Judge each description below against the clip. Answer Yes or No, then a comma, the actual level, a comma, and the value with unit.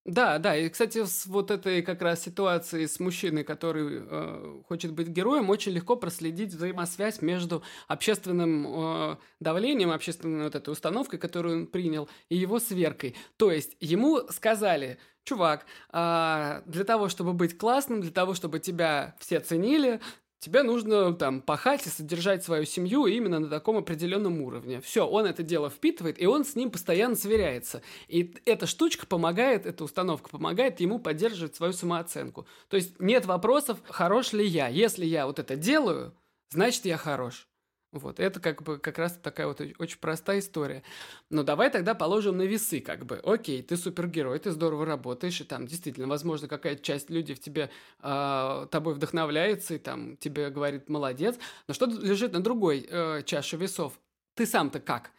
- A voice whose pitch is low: No, medium, 170 Hz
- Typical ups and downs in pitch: Yes, average, 4.3 semitones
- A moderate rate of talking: No, fast, 165 wpm